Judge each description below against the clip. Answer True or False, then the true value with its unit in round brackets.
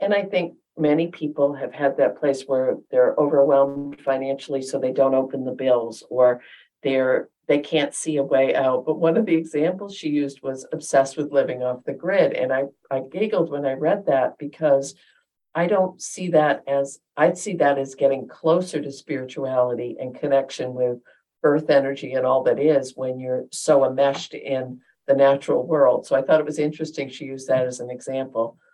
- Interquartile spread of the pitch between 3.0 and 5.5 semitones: False (2.4 semitones)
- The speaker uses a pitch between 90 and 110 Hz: False (140 Hz)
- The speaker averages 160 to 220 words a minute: True (190 wpm)